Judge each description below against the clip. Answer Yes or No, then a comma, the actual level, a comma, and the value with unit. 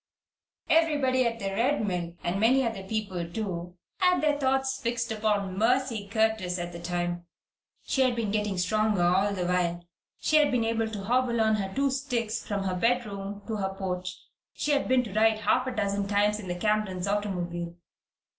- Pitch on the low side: No, high, 210 Hz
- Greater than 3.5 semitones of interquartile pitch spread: Yes, average, 4.2 semitones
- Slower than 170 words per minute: No, average, 185 wpm